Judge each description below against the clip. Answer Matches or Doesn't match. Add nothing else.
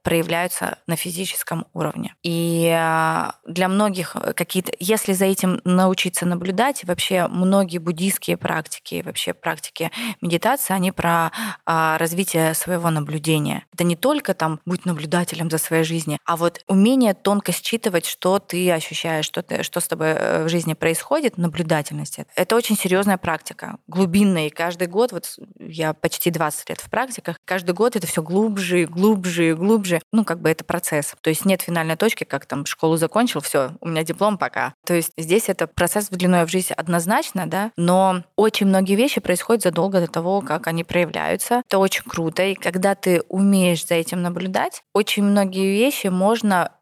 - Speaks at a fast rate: Matches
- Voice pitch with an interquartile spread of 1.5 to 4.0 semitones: Matches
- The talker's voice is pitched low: Doesn't match